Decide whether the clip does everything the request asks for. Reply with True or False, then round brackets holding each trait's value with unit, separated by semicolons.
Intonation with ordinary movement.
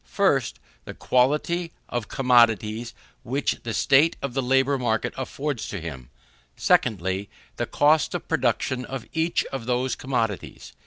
True (3.5 semitones)